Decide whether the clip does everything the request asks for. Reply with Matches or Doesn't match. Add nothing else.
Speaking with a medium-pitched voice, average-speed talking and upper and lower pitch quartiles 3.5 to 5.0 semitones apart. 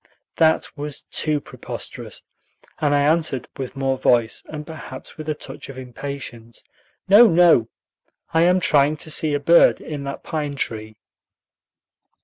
Doesn't match